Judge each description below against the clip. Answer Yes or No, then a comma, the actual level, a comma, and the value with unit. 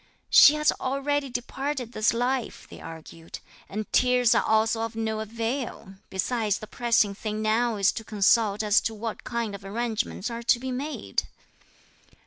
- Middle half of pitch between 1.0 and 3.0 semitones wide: Yes, narrow, 2.5 semitones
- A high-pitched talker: Yes, high, 230 Hz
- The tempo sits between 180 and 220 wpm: No, average, 160 wpm